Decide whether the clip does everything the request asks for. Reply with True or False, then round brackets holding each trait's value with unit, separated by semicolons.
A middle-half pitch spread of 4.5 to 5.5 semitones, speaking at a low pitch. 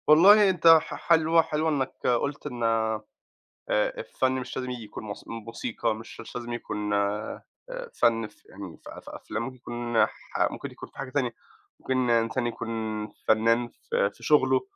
True (4.9 semitones; 120 Hz)